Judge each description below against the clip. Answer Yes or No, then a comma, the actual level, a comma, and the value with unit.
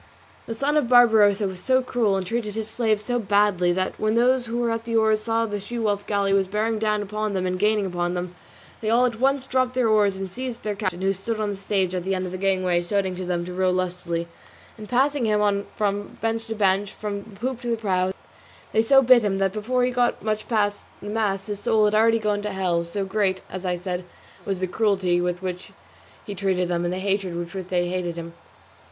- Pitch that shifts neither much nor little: Yes, average, 3.2 semitones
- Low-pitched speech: No, high, 205 Hz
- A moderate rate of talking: No, fast, 245 wpm